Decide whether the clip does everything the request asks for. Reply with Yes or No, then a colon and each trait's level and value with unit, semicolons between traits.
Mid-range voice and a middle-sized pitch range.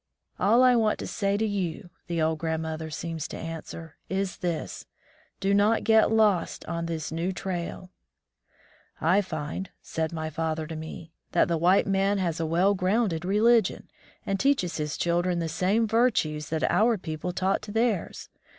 Yes: medium, 180 Hz; average, 4.0 semitones